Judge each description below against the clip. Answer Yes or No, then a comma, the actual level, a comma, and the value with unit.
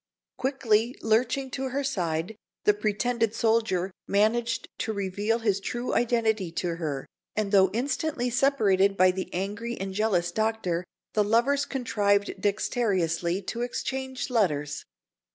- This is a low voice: No, high, 215 Hz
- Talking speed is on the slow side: Yes, slow, 130 wpm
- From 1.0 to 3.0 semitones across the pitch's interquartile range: No, average, 3.9 semitones